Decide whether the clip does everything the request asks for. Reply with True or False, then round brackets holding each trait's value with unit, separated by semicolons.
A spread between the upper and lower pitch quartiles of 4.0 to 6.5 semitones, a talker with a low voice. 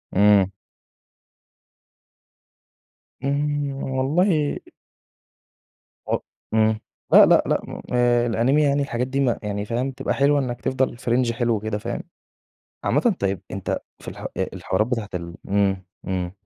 True (4.7 semitones; 120 Hz)